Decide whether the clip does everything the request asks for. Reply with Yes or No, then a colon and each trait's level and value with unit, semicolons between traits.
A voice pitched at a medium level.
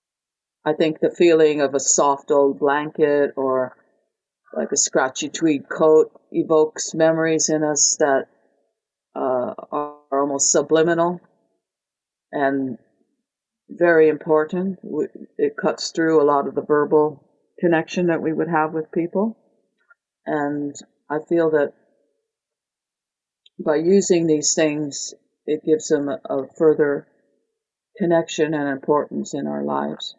Yes: medium, 155 Hz